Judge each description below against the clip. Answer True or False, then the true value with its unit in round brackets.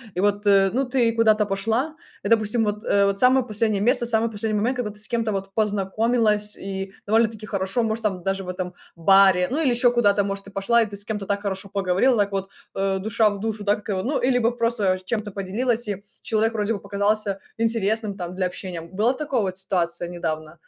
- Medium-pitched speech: False (205 Hz)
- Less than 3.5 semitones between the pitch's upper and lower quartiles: True (2.7 semitones)